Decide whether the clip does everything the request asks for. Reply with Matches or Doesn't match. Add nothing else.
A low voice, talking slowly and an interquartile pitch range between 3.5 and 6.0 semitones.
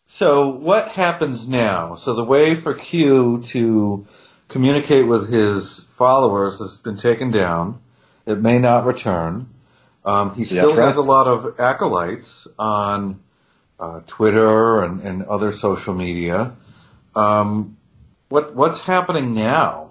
Matches